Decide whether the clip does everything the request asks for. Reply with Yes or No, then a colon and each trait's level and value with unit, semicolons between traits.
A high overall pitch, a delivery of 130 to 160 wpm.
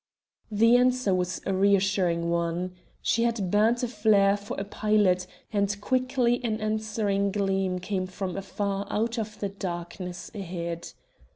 Yes: high, 200 Hz; average, 145 wpm